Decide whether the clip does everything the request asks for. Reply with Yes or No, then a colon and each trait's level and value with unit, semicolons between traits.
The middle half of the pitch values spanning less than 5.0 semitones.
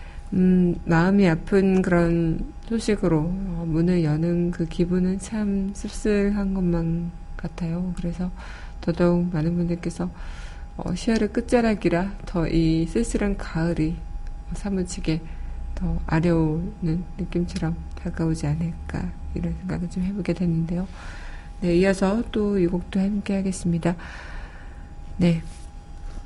Yes: narrow, 2.6 semitones